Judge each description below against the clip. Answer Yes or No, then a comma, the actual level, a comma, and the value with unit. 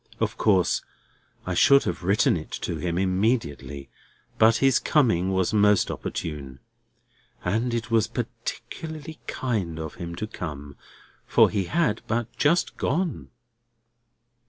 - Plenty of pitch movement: Yes, wide, 5.8 semitones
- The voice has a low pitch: Yes, low, 100 Hz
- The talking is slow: Yes, slow, 130 wpm